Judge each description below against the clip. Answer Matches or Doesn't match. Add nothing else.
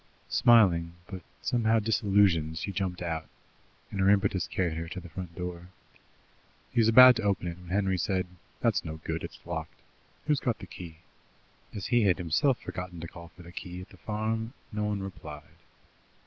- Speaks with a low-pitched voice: Matches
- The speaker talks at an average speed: Matches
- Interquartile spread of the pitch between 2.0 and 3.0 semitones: Doesn't match